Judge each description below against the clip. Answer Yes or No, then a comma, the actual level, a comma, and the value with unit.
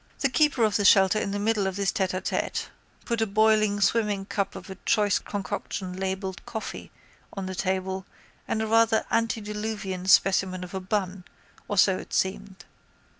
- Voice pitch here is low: No, high, 200 Hz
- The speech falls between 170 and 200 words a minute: Yes, average, 175 wpm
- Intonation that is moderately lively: No, narrow, 2.2 semitones